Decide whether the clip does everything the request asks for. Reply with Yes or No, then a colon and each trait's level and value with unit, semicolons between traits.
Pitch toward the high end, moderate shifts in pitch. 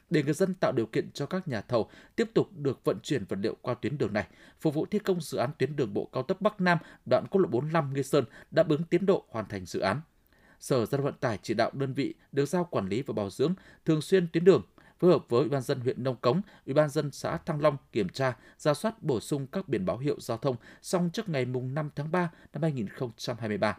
No: medium, 155 Hz; average, 4.7 semitones